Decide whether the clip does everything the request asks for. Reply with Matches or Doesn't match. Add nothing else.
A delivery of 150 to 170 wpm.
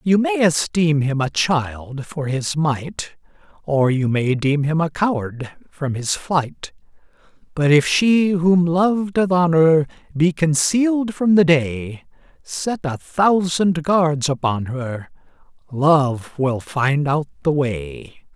Doesn't match